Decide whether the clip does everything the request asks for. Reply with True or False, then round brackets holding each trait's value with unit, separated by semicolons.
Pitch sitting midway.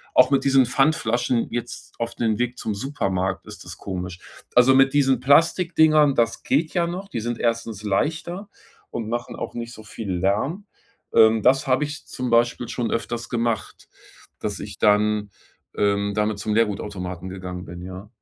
False (115 Hz)